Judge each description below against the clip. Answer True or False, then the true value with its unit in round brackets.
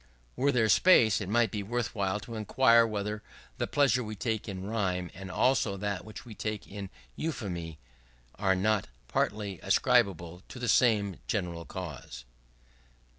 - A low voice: True (105 Hz)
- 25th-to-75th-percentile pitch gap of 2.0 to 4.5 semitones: True (3.4 semitones)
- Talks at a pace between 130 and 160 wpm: True (150 wpm)